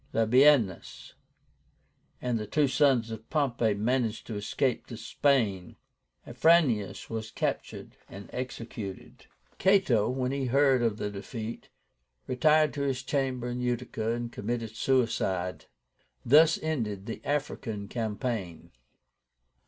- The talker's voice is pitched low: Yes, low, 120 Hz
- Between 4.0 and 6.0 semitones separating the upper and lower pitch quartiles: No, average, 3.6 semitones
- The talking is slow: Yes, slow, 115 wpm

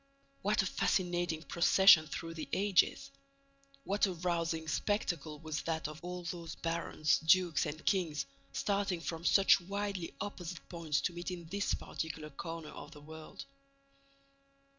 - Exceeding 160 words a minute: No, average, 140 wpm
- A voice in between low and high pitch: Yes, medium, 170 Hz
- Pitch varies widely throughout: No, average, 2.7 semitones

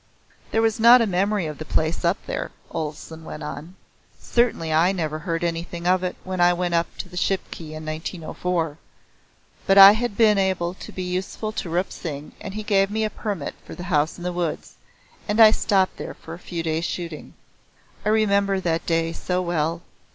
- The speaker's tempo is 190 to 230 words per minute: Yes, average, 200 wpm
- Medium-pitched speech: Yes, medium, 180 Hz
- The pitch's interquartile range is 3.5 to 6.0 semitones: No, average, 3.1 semitones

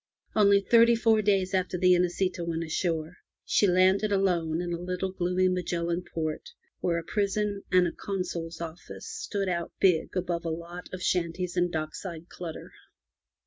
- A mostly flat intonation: Yes, narrow, 2.3 semitones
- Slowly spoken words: No, average, 165 wpm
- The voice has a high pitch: No, medium, 180 Hz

